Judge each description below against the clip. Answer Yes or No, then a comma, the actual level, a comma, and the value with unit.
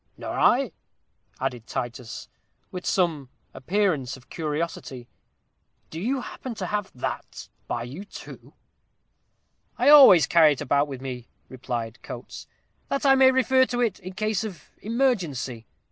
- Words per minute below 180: Yes, average, 140 wpm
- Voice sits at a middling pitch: Yes, medium, 170 Hz